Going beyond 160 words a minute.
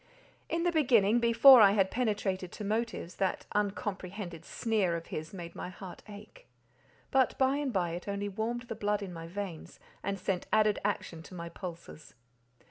Yes: average, 175 wpm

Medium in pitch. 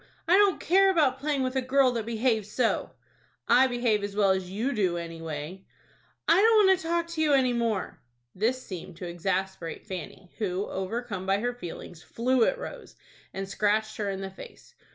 No: high, 220 Hz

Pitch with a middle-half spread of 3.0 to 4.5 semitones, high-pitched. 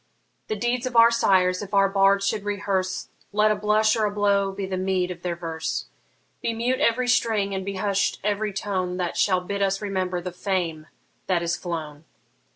No: narrow, 2.4 semitones; high, 195 Hz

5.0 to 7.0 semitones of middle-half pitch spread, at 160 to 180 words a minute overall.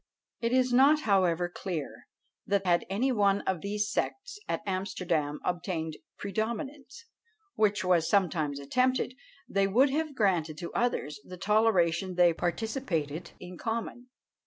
No: average, 5.3 semitones; slow, 135 wpm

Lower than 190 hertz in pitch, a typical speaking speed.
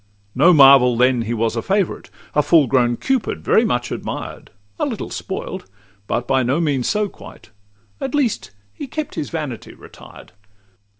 Yes: medium, 140 Hz; average, 165 wpm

